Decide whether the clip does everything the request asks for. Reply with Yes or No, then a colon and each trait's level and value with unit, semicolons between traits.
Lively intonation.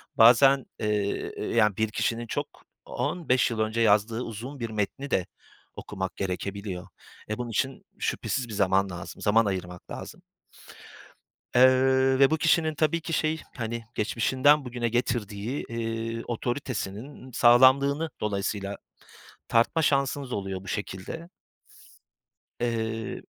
No: average, 4.2 semitones